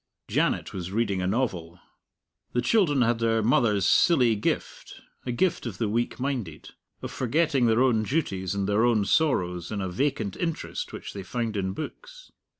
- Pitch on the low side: Yes, low, 115 Hz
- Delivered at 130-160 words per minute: No, average, 170 wpm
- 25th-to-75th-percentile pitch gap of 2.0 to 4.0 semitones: No, average, 5.1 semitones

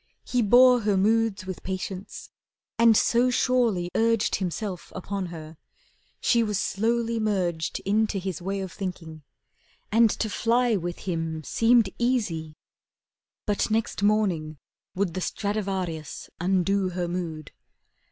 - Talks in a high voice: Yes, high, 195 Hz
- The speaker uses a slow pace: Yes, slow, 125 wpm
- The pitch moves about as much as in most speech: Yes, average, 4.2 semitones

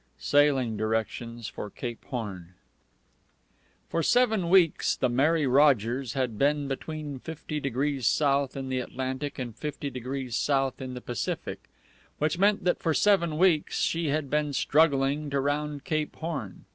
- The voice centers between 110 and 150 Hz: Yes, medium, 140 Hz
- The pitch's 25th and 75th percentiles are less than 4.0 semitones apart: Yes, average, 3.2 semitones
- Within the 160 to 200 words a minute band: No, average, 145 wpm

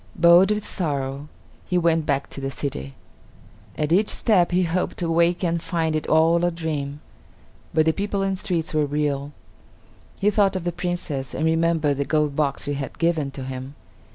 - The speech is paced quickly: No, average, 185 wpm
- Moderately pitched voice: Yes, medium, 160 Hz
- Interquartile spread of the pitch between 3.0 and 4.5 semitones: Yes, average, 3.4 semitones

